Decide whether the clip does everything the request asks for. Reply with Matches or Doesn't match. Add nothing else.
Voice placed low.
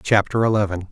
Matches